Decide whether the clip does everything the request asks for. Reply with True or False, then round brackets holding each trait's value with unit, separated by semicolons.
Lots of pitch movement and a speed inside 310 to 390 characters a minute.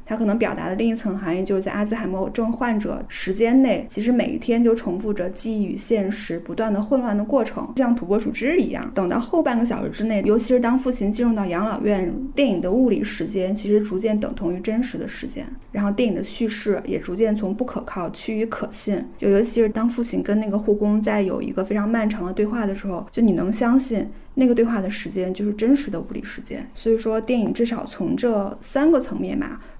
False (2.9 semitones; 350 characters per minute)